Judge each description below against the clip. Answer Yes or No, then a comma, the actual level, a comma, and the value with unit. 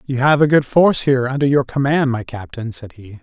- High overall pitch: No, low, 130 Hz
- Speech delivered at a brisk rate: Yes, fast, 240 wpm